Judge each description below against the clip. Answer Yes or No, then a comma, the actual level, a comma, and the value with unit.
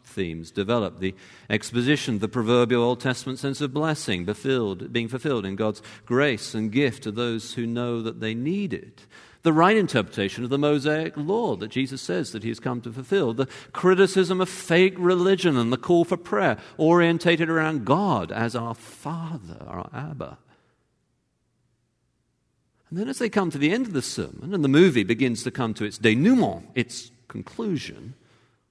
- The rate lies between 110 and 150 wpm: No, average, 175 wpm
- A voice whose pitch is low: Yes, low, 130 Hz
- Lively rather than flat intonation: Yes, wide, 6.0 semitones